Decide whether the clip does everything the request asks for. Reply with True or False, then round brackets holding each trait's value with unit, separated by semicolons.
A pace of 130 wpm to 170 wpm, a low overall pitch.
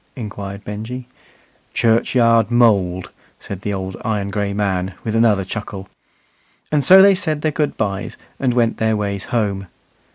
True (150 wpm; 105 Hz)